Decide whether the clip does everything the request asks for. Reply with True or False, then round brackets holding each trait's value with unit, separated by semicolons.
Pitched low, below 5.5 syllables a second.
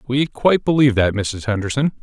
False (125 Hz; 6.0 syllables/s)